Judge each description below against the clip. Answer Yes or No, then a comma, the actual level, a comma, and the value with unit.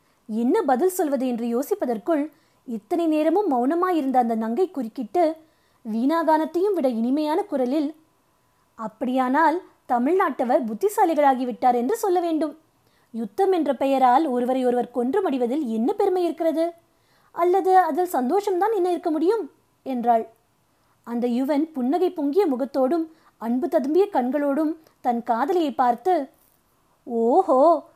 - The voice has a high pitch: Yes, very high, 300 Hz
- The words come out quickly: No, average, 105 wpm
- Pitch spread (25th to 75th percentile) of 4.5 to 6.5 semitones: Yes, average, 5.3 semitones